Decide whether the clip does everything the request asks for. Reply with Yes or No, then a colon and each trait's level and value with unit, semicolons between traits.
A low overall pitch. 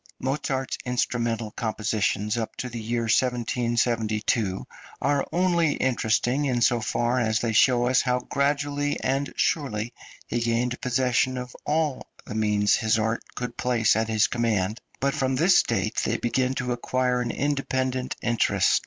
Yes: low, 125 Hz